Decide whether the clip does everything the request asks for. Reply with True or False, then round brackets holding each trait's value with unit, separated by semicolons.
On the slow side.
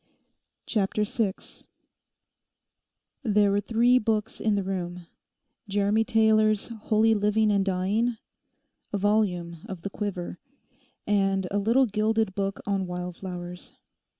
True (110 wpm)